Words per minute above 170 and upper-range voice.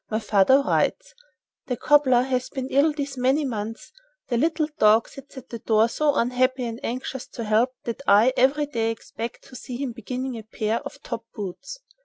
Yes: average, 190 wpm; very high, 250 Hz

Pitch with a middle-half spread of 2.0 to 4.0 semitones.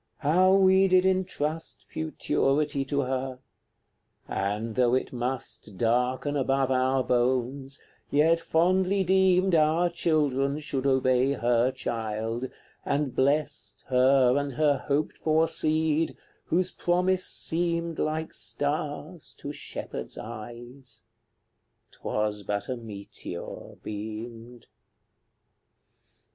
No: average, 4.7 semitones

